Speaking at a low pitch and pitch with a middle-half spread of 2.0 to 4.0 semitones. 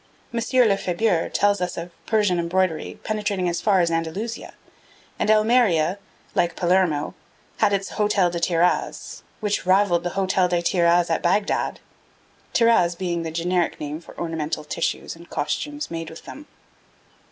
No: medium, 180 Hz; average, 3.3 semitones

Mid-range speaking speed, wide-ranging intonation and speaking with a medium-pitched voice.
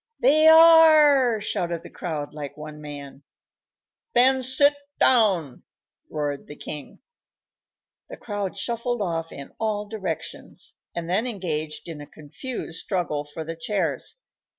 No: slow, 130 wpm; wide, 8.0 semitones; medium, 180 Hz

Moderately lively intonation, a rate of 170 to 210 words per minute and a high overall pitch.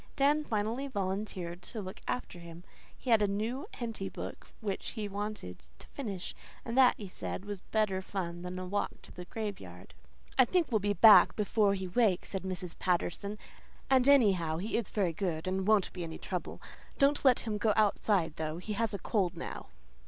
Yes: average, 3.4 semitones; average, 190 wpm; high, 205 Hz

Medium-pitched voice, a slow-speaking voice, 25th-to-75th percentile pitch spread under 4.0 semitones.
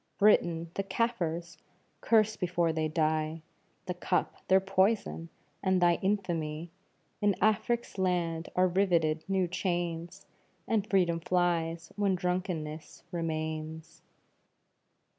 Yes: medium, 175 Hz; slow, 105 wpm; average, 2.7 semitones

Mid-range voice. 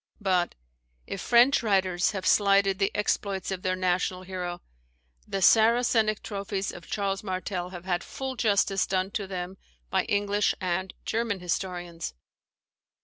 No: high, 195 Hz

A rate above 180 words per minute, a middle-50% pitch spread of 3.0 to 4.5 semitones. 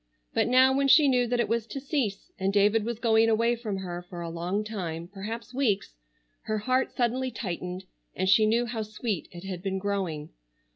Yes: average, 200 wpm; average, 4.1 semitones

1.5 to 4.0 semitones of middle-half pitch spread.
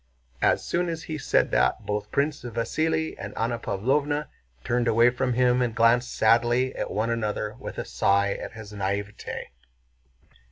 Yes: average, 3.7 semitones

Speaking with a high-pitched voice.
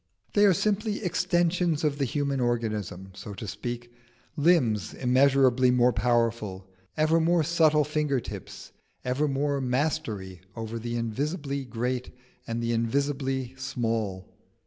No: low, 130 Hz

